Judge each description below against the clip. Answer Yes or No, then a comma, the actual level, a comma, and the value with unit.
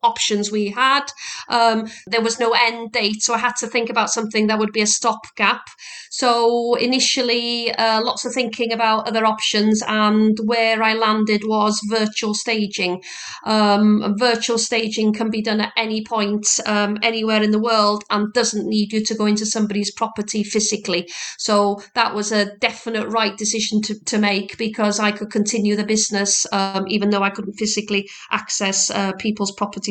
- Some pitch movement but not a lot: No, narrow, 1.6 semitones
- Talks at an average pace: Yes, average, 175 wpm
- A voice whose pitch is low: No, high, 215 Hz